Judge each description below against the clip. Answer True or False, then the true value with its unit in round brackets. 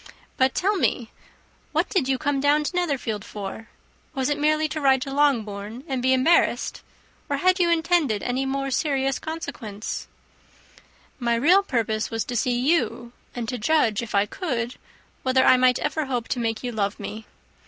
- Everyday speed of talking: True (175 wpm)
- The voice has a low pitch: False (260 Hz)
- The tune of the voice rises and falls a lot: False (4.4 semitones)